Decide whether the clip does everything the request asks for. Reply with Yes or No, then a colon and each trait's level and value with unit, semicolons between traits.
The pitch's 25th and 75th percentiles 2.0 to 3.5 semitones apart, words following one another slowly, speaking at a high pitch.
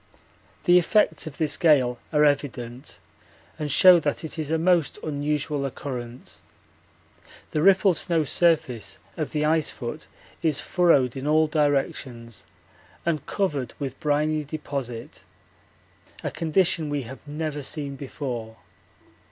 No: average, 2.9 semitones; slow, 125 wpm; medium, 150 Hz